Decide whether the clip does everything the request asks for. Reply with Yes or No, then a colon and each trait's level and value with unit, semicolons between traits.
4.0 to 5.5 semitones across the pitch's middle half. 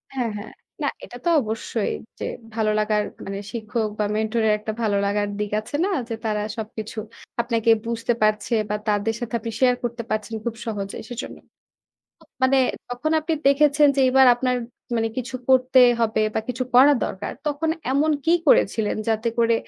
No: average, 3.0 semitones